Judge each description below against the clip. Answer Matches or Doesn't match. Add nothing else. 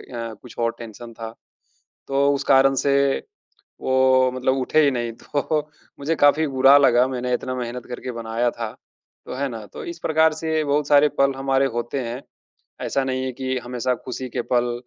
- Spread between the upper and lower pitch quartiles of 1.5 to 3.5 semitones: Matches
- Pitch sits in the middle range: Doesn't match